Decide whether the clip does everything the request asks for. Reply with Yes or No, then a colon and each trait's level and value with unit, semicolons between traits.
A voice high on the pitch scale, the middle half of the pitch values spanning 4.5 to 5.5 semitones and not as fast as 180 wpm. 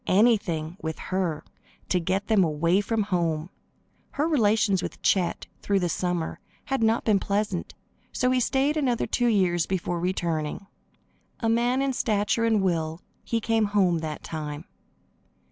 Yes: high, 195 Hz; average, 4.9 semitones; average, 150 wpm